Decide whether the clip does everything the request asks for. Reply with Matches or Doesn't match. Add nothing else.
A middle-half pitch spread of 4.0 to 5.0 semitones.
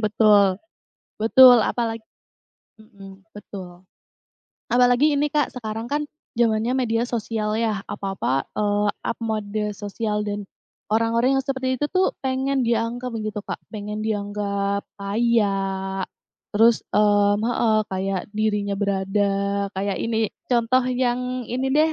Doesn't match